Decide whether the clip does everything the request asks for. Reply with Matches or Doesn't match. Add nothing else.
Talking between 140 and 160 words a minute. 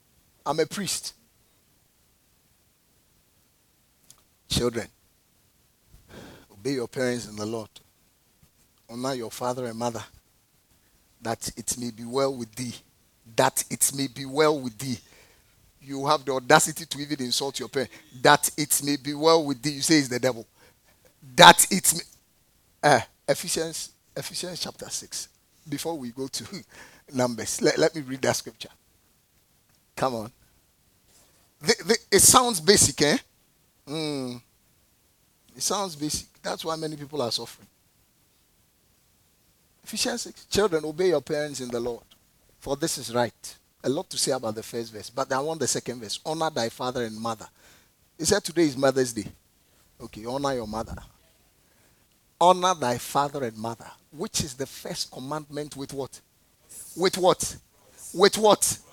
Matches